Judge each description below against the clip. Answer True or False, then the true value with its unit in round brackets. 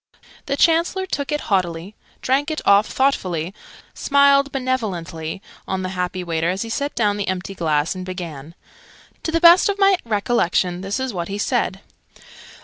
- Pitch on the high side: True (200 Hz)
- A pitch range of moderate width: False (7.6 semitones)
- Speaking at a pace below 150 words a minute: False (165 wpm)